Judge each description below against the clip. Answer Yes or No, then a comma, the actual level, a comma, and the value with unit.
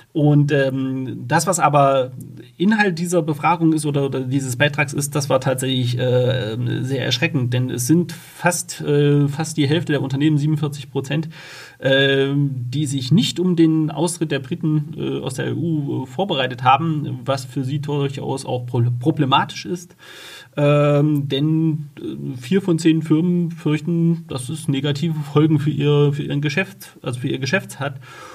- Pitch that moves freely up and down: No, average, 2.9 semitones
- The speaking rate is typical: Yes, average, 160 wpm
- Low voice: No, medium, 145 Hz